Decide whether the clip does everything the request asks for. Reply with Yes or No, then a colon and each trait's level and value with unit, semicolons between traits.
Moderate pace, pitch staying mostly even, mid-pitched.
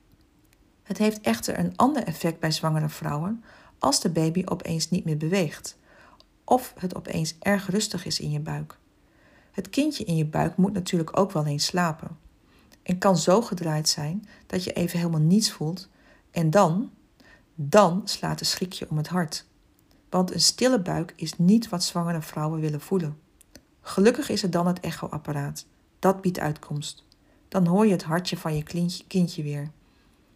No: average, 170 wpm; average, 3.7 semitones; medium, 175 Hz